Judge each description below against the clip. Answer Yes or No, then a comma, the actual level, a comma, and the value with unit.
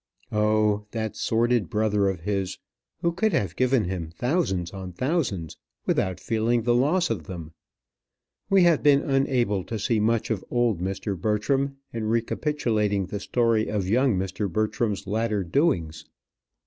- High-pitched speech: No, low, 110 Hz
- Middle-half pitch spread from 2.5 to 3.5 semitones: No, average, 4.1 semitones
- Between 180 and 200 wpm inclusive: No, average, 150 wpm